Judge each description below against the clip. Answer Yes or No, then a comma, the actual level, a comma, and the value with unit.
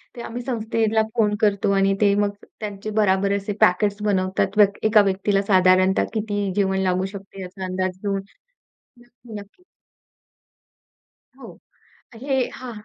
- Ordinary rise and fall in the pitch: No, narrow, 2.2 semitones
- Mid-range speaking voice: No, high, 200 Hz